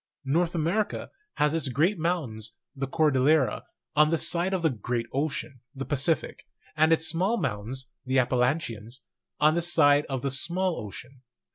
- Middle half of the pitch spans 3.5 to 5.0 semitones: Yes, average, 4.2 semitones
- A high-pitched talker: No, medium, 145 Hz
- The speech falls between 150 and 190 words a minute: Yes, average, 155 wpm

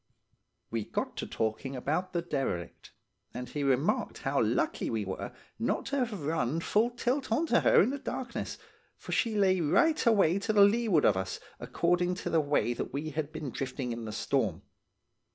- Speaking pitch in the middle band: Yes, medium, 165 Hz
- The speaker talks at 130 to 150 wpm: No, average, 180 wpm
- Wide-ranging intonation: Yes, wide, 8.4 semitones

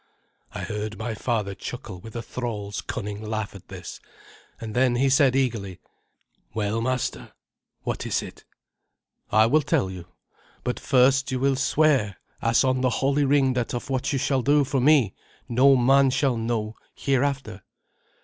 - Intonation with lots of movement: No, average, 3.7 semitones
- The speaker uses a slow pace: No, average, 160 wpm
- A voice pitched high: No, low, 125 Hz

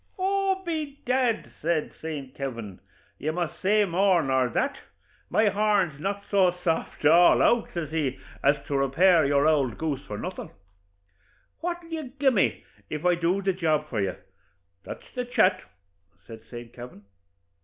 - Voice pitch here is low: No, medium, 170 Hz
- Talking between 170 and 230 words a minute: No, average, 155 wpm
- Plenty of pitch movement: Yes, wide, 7.1 semitones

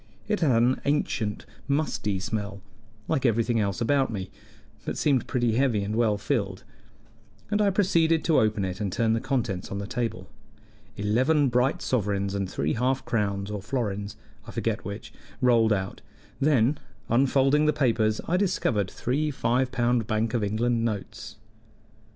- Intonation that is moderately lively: Yes, average, 4.5 semitones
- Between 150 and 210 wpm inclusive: Yes, average, 155 wpm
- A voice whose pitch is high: No, low, 115 Hz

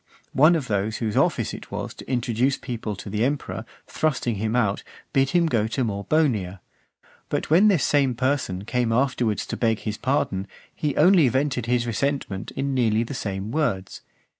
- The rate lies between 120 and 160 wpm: No, average, 175 wpm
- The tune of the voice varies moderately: Yes, average, 4.5 semitones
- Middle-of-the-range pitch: No, low, 120 Hz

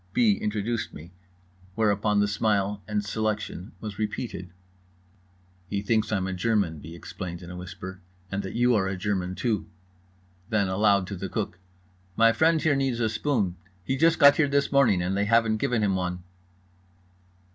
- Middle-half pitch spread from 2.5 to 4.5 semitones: Yes, average, 3.5 semitones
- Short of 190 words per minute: Yes, average, 170 wpm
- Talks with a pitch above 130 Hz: No, low, 105 Hz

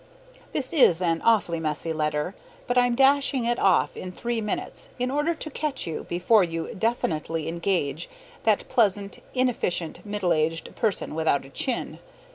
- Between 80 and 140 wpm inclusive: No, average, 155 wpm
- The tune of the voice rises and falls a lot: Yes, wide, 7.0 semitones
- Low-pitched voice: No, high, 195 Hz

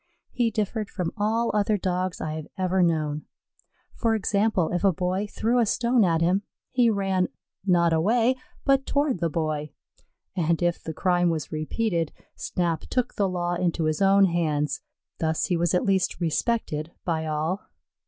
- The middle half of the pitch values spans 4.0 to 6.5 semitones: Yes, average, 4.3 semitones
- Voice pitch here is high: No, medium, 180 Hz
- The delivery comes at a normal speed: Yes, average, 165 wpm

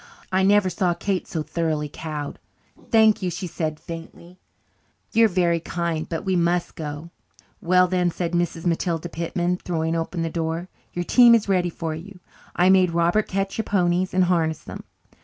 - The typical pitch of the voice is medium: Yes, medium, 175 Hz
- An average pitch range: No, narrow, 2.1 semitones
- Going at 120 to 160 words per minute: No, average, 175 wpm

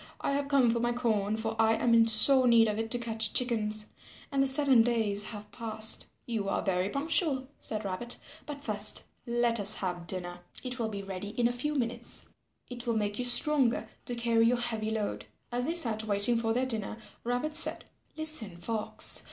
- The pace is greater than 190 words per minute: Yes, average, 200 wpm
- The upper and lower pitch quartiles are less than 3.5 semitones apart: Yes, narrow, 2.6 semitones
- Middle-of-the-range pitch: No, high, 230 Hz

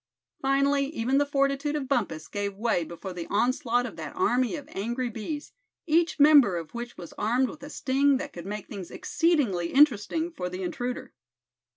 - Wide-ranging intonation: Yes, wide, 5.9 semitones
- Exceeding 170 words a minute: Yes, average, 180 wpm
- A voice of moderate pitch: No, very high, 250 Hz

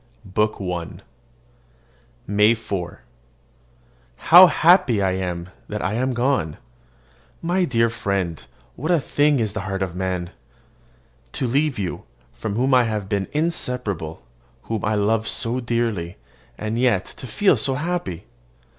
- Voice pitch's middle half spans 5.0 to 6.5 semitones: Yes, average, 5.3 semitones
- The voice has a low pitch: Yes, low, 110 Hz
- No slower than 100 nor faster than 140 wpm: Yes, slow, 135 wpm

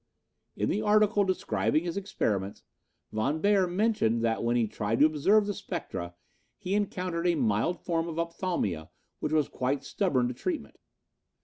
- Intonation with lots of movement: Yes, wide, 8.7 semitones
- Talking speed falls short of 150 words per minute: No, average, 155 wpm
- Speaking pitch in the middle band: Yes, medium, 165 Hz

